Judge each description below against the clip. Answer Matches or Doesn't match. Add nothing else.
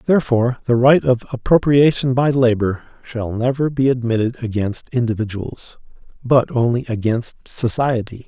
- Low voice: Matches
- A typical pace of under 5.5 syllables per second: Matches